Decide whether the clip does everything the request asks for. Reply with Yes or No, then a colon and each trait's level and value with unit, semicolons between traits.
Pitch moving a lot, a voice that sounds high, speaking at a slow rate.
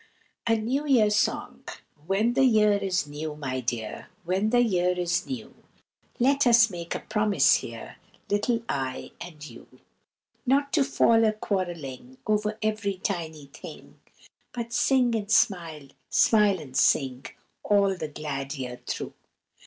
No: wide, 6.9 semitones; high, 200 Hz; average, 145 wpm